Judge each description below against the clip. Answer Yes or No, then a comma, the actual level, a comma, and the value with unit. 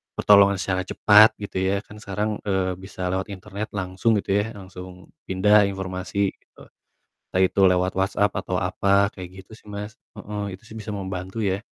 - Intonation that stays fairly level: Yes, narrow, 1.7 semitones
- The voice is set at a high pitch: No, low, 100 Hz